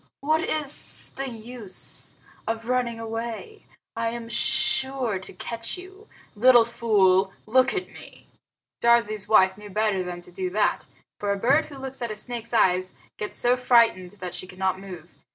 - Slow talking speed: No, average, 165 wpm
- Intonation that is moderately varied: Yes, average, 4.5 semitones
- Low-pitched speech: No, high, 230 Hz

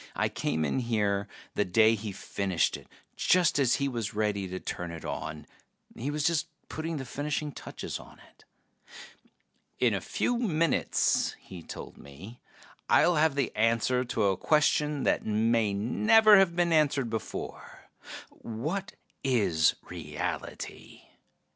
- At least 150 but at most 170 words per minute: No, average, 140 wpm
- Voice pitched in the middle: No, low, 120 Hz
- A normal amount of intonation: No, wide, 7.0 semitones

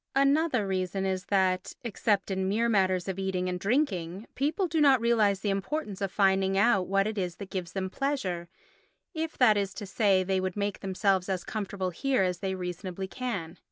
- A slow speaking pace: No, average, 190 wpm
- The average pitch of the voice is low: No, high, 195 Hz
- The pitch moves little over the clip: No, average, 3.0 semitones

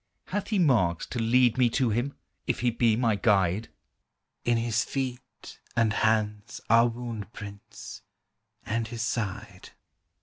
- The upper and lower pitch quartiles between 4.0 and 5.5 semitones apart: No, narrow, 2.4 semitones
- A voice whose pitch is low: Yes, low, 115 Hz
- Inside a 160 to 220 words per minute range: No, average, 140 wpm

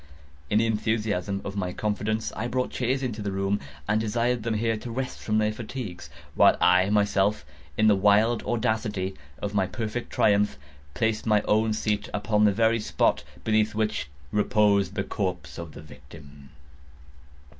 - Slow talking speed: No, average, 165 wpm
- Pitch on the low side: Yes, low, 105 Hz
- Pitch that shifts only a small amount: Yes, narrow, 2.1 semitones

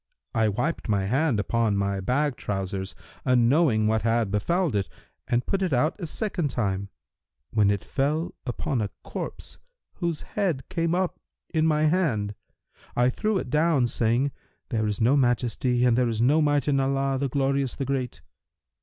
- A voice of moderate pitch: No, low, 130 Hz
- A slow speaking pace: No, average, 170 wpm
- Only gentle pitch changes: No, wide, 5.5 semitones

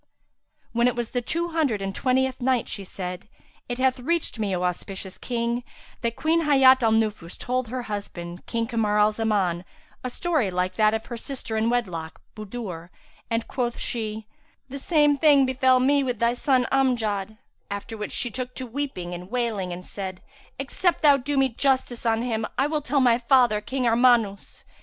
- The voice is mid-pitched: No, high, 235 Hz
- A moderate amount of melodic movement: Yes, average, 3.8 semitones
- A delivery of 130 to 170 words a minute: No, average, 185 wpm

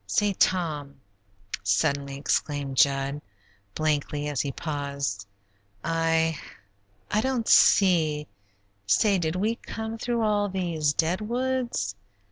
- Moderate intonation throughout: No, wide, 6.4 semitones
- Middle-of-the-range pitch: Yes, medium, 160 Hz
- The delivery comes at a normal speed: No, slow, 105 wpm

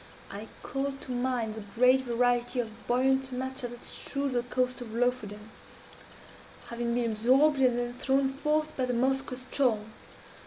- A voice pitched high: Yes, very high, 250 Hz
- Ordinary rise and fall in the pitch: No, narrow, 2.0 semitones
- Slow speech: No, average, 155 wpm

